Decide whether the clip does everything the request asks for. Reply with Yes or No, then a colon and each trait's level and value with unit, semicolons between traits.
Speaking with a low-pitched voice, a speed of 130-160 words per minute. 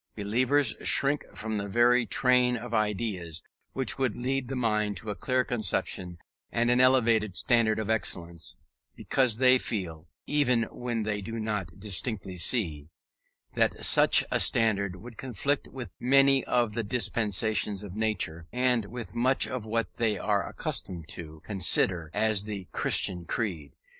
Yes: low, 110 Hz; average, 150 wpm